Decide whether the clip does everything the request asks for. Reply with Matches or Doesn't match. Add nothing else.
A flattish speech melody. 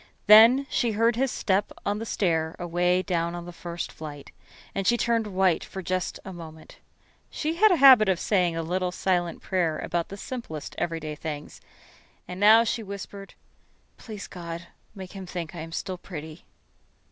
Doesn't match